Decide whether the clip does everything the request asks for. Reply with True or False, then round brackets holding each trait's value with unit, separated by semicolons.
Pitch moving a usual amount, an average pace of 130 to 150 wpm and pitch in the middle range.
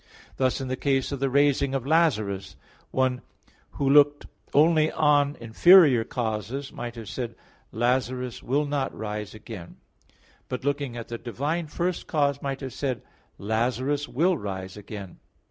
False (3.8 semitones; 145 wpm; 130 Hz)